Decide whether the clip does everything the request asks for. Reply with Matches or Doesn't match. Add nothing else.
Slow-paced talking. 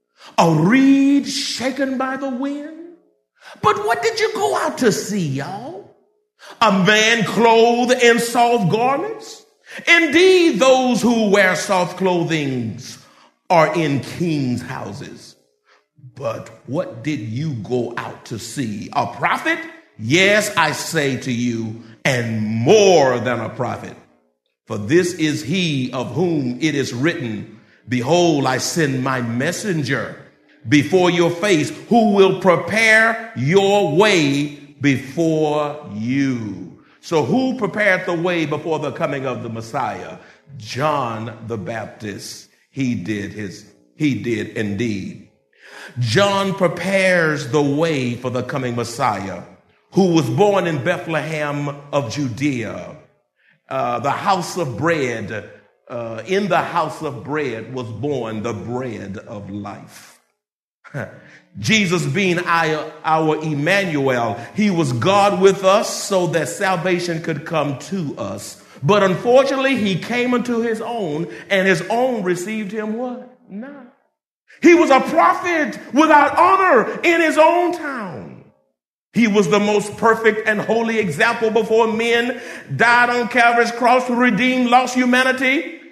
Matches